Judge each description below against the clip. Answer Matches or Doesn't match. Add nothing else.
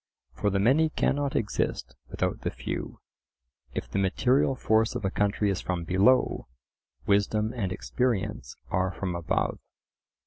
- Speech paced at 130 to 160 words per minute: Matches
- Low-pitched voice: Matches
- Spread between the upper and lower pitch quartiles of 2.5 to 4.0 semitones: Doesn't match